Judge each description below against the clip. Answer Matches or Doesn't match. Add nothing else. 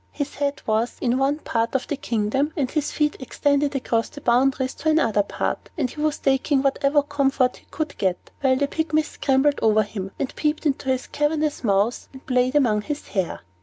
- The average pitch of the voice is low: Doesn't match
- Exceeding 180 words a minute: Matches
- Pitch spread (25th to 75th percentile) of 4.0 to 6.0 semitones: Doesn't match